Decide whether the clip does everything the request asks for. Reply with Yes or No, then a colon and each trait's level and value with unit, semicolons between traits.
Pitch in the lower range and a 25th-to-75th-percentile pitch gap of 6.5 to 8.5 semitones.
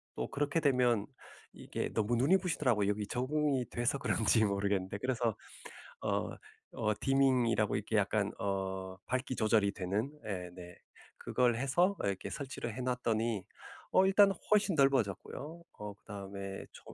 No: low, 120 Hz; average, 5.3 semitones